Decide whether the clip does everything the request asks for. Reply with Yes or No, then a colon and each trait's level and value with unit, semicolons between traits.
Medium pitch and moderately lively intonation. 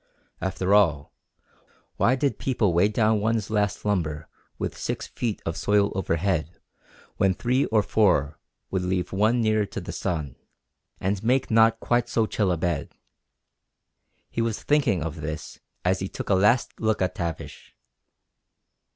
No: low, 100 Hz; average, 3.9 semitones